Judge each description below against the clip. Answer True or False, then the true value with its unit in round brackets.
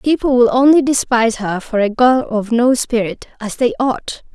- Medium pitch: False (240 Hz)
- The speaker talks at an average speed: True (180 wpm)